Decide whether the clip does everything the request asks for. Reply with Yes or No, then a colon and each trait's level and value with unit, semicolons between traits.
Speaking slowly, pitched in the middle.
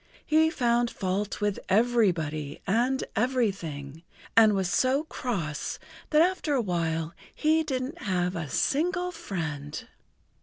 No: slow, 120 wpm; high, 215 Hz